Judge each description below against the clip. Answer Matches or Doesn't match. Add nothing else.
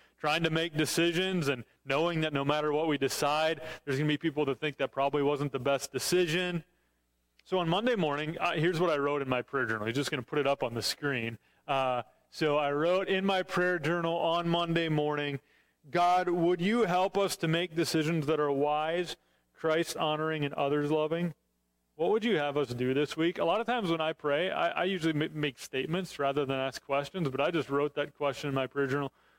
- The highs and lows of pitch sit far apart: Doesn't match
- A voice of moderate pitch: Matches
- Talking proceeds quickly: Matches